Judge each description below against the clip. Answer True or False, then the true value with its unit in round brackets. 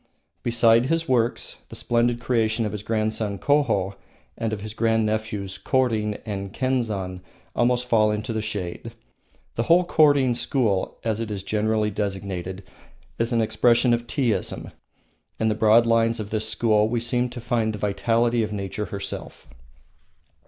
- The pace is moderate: True (155 wpm)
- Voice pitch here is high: False (110 Hz)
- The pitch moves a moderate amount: False (2.1 semitones)